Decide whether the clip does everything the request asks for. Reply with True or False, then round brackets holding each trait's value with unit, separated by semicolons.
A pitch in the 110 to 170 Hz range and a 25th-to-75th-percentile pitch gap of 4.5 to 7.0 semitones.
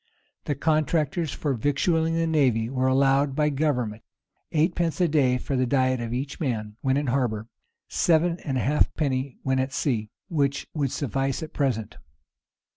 False (140 Hz; 3.1 semitones)